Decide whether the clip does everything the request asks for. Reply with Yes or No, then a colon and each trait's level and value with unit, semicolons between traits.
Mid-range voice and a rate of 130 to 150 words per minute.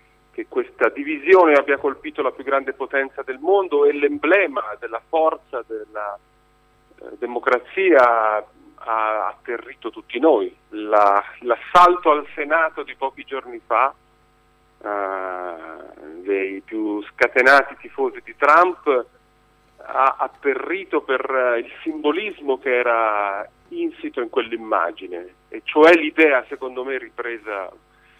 No: medium, 145 Hz; slow, 115 wpm